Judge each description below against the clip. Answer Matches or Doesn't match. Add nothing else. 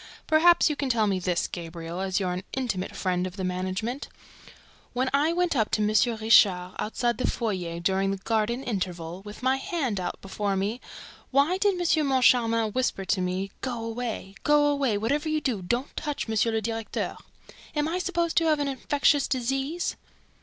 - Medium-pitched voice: Doesn't match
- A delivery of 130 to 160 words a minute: Doesn't match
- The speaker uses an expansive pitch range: Matches